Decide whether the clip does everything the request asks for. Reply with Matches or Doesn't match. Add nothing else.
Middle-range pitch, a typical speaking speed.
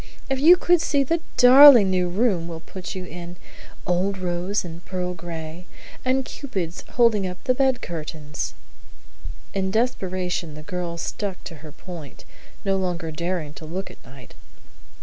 Matches